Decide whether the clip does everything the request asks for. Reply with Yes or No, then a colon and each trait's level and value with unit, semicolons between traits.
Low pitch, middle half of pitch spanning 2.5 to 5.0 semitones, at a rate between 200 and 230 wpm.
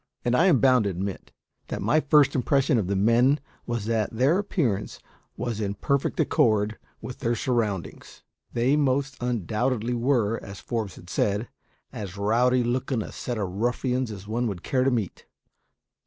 No: low, 120 Hz; average, 3.6 semitones; average, 170 wpm